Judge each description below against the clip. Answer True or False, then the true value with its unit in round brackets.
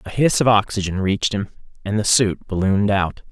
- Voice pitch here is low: True (100 Hz)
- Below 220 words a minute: True (200 wpm)